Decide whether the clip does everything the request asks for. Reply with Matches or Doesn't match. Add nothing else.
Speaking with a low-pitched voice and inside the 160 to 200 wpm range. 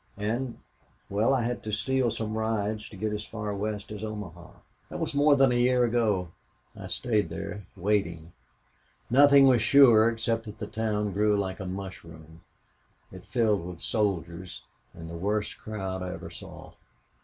Matches